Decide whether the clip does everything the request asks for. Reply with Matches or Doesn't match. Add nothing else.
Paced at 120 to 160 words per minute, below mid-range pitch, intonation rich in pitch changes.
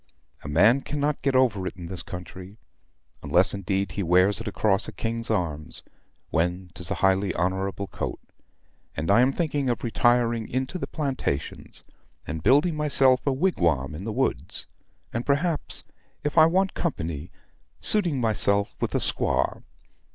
Matches